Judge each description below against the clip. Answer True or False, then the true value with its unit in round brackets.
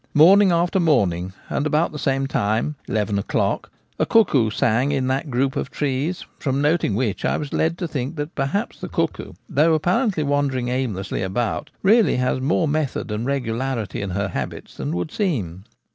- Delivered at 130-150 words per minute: False (185 wpm)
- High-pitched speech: False (135 Hz)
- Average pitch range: False (6.0 semitones)